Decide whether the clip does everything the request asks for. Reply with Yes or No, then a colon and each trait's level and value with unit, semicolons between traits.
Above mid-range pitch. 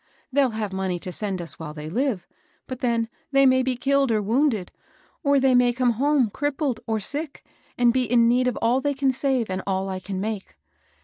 Yes: high, 240 Hz